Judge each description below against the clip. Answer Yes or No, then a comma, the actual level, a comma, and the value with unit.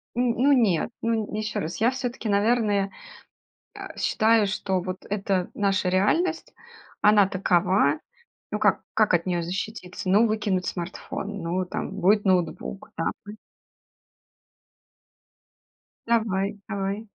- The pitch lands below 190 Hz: No, high, 200 Hz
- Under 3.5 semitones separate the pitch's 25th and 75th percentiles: Yes, average, 2.8 semitones